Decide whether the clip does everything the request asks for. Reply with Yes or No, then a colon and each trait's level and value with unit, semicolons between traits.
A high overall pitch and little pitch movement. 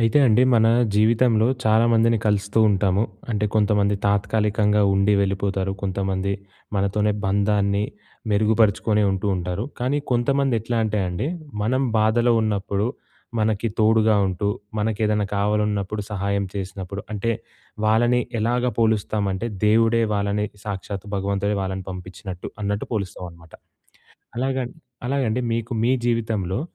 No: low, 105 Hz; narrow, 2.1 semitones